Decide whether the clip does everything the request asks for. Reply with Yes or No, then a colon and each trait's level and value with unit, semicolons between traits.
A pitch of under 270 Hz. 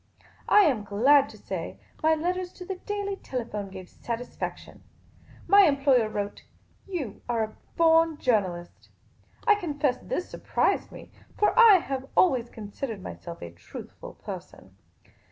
No: very high, 275 Hz